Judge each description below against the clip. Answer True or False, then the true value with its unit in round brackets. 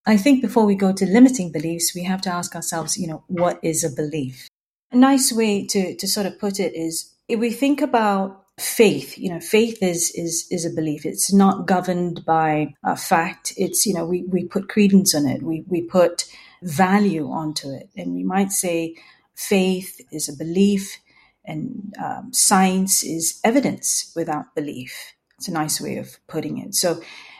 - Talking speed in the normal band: True (190 wpm)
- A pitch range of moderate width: True (3.6 semitones)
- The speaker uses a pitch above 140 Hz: True (185 Hz)